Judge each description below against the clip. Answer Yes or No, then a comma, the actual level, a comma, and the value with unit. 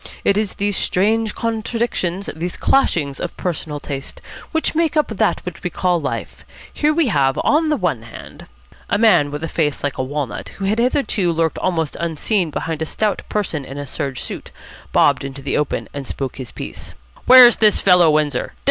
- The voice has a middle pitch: Yes, medium, 175 Hz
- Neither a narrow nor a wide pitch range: No, wide, 6.8 semitones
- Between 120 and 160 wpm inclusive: No, average, 190 wpm